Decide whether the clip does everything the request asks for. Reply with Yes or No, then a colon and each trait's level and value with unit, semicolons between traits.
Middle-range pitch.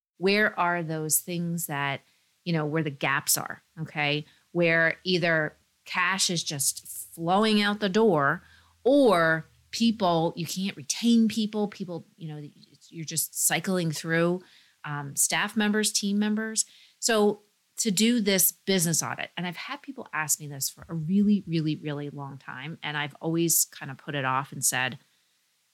Yes: medium, 165 Hz